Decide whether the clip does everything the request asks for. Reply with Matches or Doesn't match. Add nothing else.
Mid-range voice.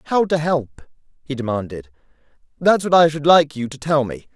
Matches